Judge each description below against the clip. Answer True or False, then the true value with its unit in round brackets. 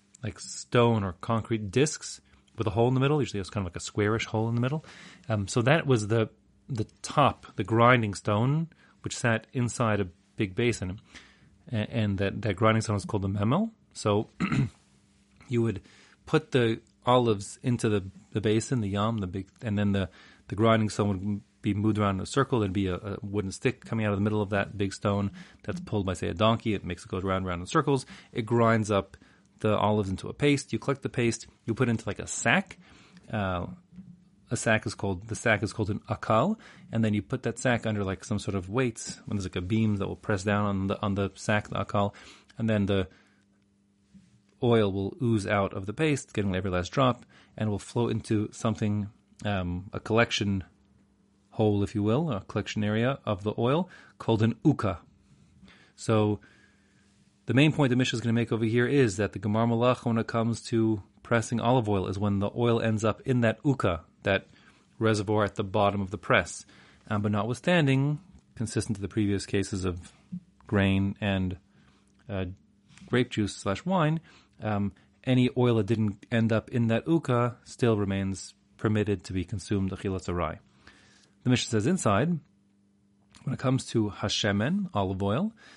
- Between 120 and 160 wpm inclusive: False (200 wpm)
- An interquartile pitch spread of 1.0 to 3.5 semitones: True (2.9 semitones)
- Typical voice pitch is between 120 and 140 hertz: False (110 Hz)